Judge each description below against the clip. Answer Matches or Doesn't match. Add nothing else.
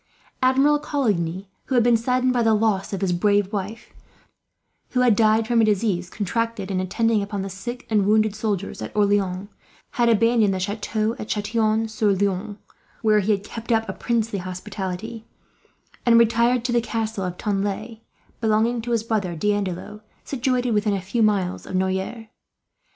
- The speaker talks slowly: Doesn't match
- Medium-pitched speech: Doesn't match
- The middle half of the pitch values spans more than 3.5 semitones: Doesn't match